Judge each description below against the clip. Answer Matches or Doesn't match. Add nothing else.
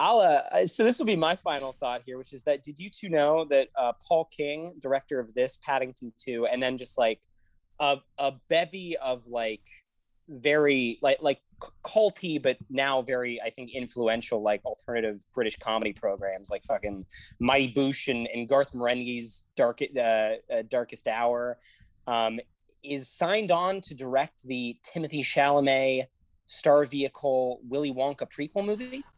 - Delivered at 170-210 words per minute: Doesn't match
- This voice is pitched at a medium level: Doesn't match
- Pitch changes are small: Doesn't match